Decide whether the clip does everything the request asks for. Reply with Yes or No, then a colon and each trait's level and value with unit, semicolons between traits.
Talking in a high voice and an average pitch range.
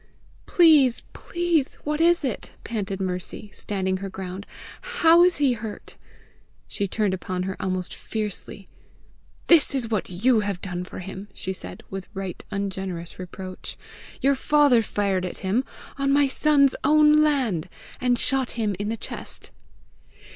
No: high, 215 Hz; wide, 6.7 semitones